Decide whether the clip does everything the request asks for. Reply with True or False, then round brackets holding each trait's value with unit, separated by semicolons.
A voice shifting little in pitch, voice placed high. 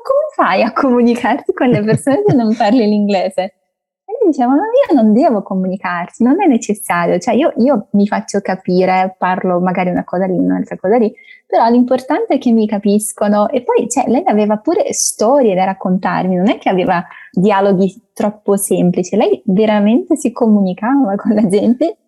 False (5.6 semitones; 215 Hz)